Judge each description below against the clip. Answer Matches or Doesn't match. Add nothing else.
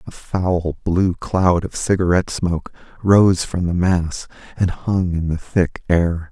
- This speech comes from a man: Matches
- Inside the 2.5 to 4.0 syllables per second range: Matches